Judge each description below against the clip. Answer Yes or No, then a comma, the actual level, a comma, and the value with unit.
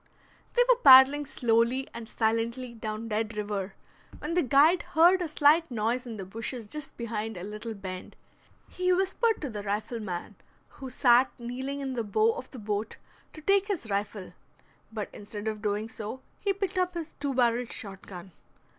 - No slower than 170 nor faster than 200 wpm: Yes, average, 175 wpm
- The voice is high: Yes, high, 235 Hz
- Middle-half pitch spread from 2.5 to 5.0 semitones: No, wide, 5.6 semitones